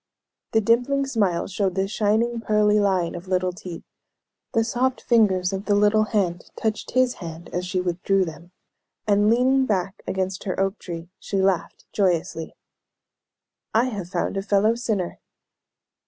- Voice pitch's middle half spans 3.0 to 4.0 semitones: Yes, average, 3.4 semitones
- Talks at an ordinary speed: Yes, average, 155 wpm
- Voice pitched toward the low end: No, high, 200 Hz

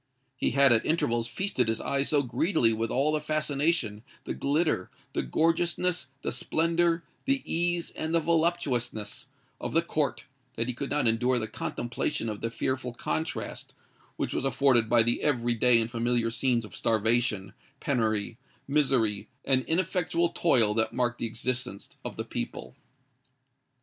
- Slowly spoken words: No, average, 155 wpm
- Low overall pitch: Yes, low, 125 Hz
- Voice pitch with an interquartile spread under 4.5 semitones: No, wide, 5.5 semitones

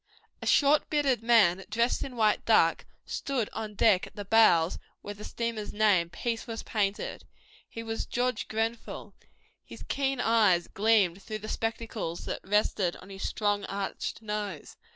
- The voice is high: Yes, high, 215 Hz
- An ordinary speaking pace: Yes, average, 155 wpm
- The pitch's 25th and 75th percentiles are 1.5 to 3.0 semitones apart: Yes, narrow, 2.5 semitones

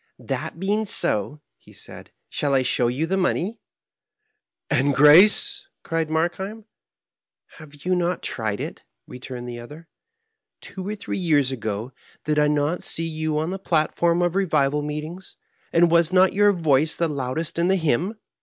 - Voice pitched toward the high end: No, medium, 160 Hz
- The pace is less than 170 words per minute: No, average, 175 wpm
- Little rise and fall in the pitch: No, average, 4.3 semitones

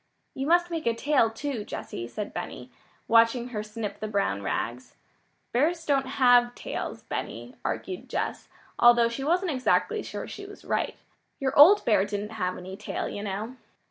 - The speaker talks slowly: No, average, 170 wpm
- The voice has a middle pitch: No, high, 240 Hz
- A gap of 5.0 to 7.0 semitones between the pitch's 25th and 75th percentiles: Yes, average, 5.3 semitones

